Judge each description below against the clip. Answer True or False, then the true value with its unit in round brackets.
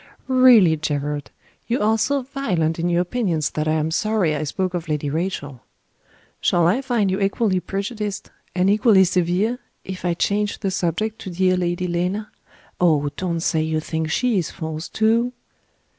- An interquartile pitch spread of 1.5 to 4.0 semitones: False (4.8 semitones)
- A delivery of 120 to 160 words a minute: False (170 wpm)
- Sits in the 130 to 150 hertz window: False (180 Hz)